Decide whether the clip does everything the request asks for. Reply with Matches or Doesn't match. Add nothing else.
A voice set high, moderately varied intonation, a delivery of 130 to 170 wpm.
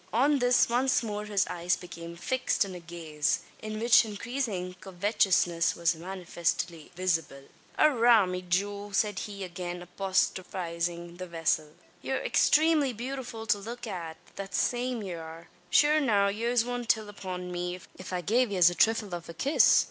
Matches